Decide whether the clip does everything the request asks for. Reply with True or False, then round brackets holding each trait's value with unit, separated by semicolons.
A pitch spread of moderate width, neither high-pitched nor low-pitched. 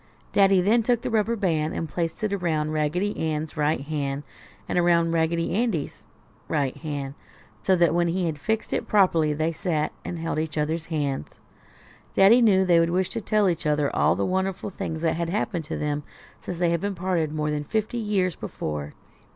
True (3.8 semitones; 165 Hz)